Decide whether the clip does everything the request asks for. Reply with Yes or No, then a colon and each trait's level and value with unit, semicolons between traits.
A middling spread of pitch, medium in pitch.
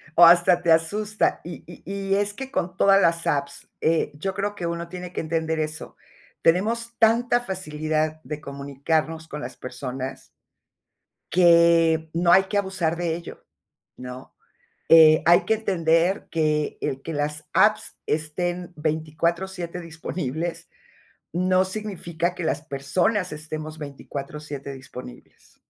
Yes: average, 3.1 semitones; medium, 165 Hz